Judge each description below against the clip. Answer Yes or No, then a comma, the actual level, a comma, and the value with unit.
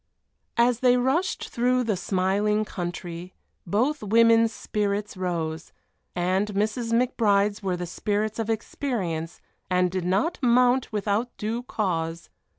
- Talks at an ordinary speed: No, slow, 125 wpm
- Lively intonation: No, average, 4.2 semitones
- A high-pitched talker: Yes, high, 210 Hz